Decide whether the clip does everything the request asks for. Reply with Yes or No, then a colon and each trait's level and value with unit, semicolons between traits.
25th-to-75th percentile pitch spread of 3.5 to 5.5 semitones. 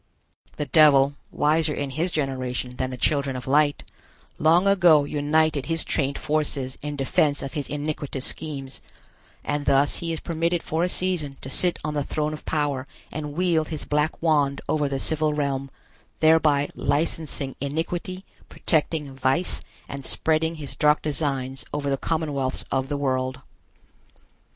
No: narrow, 2.5 semitones